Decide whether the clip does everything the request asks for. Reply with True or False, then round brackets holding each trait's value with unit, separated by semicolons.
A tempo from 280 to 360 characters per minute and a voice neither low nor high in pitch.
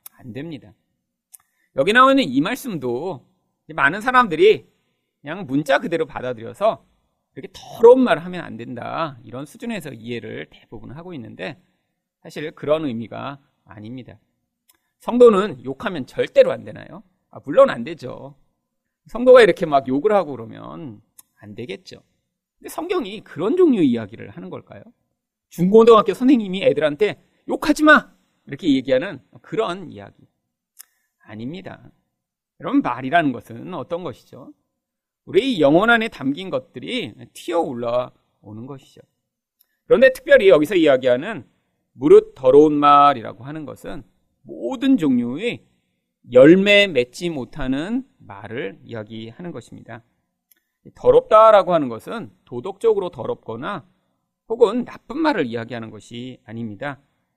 True (295 characters per minute; 165 Hz)